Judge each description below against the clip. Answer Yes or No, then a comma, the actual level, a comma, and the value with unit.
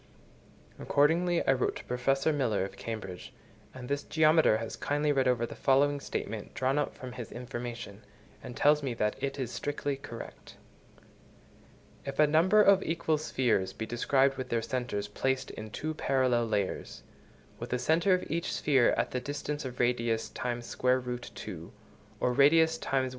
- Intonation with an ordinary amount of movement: Yes, average, 3.6 semitones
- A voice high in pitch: No, low, 130 Hz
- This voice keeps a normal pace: Yes, average, 165 wpm